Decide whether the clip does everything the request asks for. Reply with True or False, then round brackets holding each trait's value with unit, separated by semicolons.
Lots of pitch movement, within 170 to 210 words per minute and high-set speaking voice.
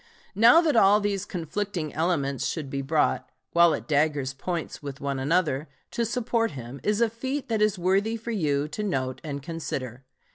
False (7.0 semitones; 180 wpm; 170 Hz)